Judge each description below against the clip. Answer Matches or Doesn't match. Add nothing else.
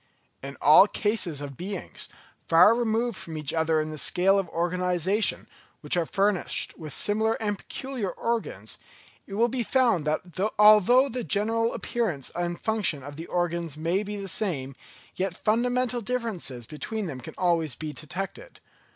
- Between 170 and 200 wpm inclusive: Doesn't match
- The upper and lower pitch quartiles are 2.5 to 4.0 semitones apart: Doesn't match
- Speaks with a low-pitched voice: Doesn't match